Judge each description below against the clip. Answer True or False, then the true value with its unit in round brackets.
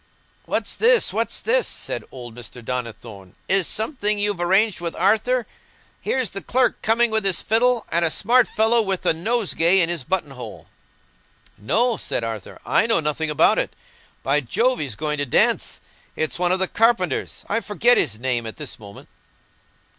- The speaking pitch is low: False (185 Hz)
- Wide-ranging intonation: True (8.7 semitones)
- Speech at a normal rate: True (170 wpm)